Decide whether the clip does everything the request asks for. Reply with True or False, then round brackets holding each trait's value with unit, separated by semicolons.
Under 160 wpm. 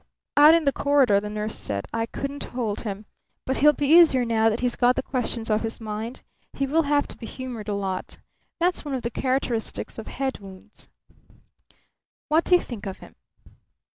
False (200 wpm)